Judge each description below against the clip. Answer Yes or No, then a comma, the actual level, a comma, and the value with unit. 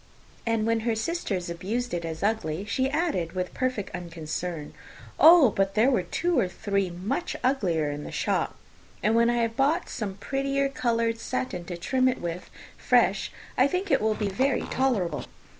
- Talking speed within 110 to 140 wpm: No, average, 175 wpm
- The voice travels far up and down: Yes, wide, 6.3 semitones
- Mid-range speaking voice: No, high, 220 Hz